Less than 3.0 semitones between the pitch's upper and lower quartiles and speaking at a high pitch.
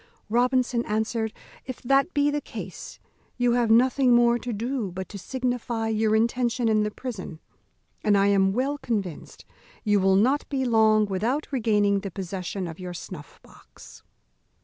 No: average, 3.8 semitones; high, 225 Hz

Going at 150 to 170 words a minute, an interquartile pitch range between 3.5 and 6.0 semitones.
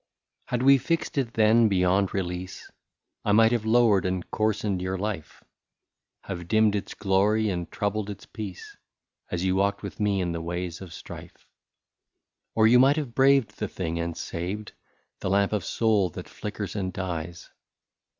No: average, 165 wpm; average, 3.1 semitones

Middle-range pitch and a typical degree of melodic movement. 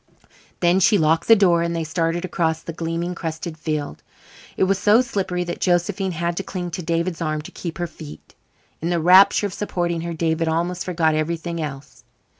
No: medium, 170 Hz; narrow, 1.8 semitones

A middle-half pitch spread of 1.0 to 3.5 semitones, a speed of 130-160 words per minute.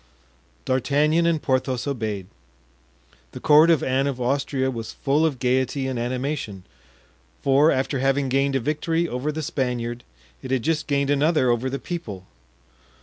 Yes: average, 2.9 semitones; average, 150 wpm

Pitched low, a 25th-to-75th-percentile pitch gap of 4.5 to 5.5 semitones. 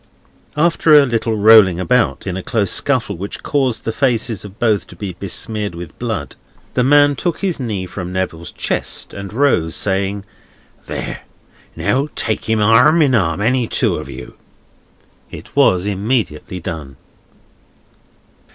Yes: low, 105 Hz; average, 5.2 semitones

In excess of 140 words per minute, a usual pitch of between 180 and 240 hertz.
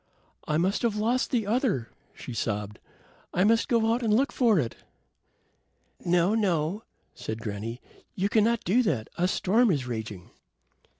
Yes: average, 155 wpm; high, 190 Hz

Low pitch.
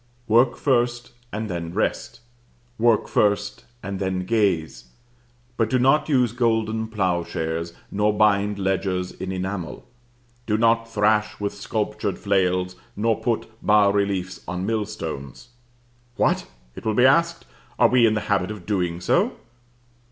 Yes: low, 105 Hz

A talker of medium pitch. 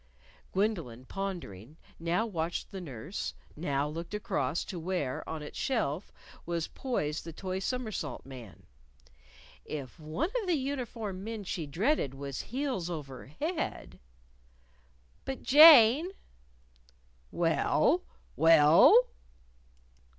Yes: medium, 175 Hz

